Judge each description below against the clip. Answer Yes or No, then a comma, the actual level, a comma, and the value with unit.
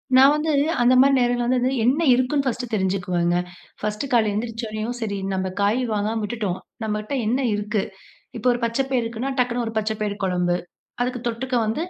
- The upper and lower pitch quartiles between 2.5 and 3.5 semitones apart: Yes, average, 3.2 semitones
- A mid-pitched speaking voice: No, high, 230 Hz